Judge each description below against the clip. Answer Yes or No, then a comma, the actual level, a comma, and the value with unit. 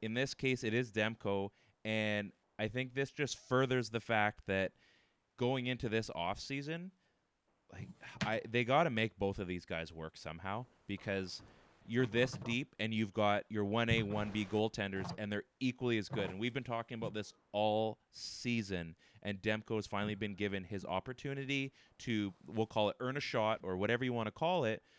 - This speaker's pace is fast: No, average, 185 wpm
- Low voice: Yes, low, 110 Hz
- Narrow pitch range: No, average, 3.3 semitones